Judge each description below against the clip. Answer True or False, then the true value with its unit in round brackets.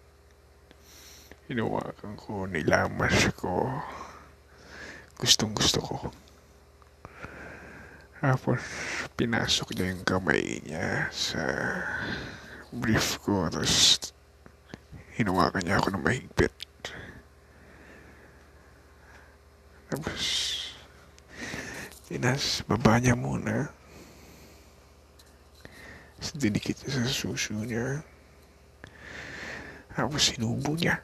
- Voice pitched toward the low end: True (80 Hz)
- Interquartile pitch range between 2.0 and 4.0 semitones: True (3.3 semitones)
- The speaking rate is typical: False (70 wpm)